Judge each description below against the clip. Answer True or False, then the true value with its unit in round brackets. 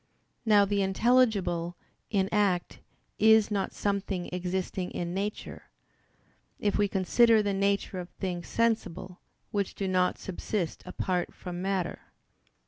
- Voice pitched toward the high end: True (195 Hz)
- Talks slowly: True (125 wpm)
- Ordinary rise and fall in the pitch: False (2.3 semitones)